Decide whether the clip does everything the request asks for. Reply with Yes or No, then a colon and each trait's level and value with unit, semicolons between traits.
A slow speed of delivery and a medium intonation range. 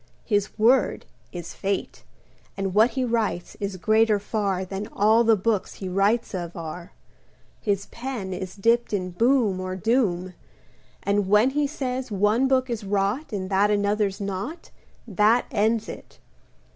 No: average, 150 wpm; average, 3.2 semitones